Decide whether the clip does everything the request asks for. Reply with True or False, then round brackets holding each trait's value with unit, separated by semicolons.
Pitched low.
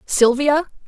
False (275 Hz)